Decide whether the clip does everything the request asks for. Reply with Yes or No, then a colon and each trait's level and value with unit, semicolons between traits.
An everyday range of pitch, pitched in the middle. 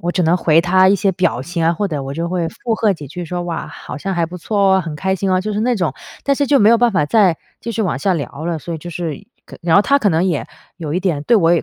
Yes: average, 3.5 semitones; medium, 175 Hz